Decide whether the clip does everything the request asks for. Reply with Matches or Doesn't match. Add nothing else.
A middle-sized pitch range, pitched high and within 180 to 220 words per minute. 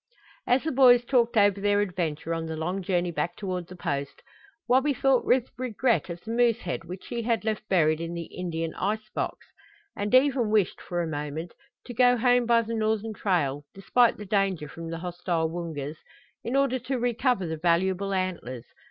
Doesn't match